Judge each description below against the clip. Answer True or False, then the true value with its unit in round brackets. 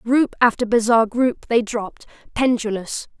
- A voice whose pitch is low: False (230 Hz)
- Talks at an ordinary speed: False (130 wpm)